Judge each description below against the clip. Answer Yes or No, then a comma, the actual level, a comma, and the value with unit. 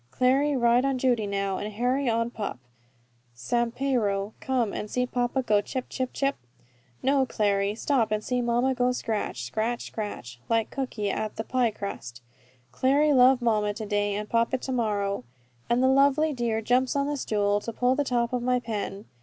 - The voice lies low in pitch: No, high, 235 Hz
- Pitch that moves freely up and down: No, average, 3.6 semitones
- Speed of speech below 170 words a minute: No, average, 185 wpm